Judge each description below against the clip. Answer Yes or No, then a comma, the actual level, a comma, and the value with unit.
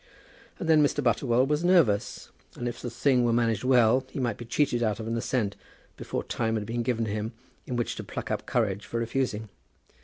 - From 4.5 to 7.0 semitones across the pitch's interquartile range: No, narrow, 2.5 semitones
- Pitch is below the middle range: Yes, low, 120 Hz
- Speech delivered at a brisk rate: Yes, fast, 210 wpm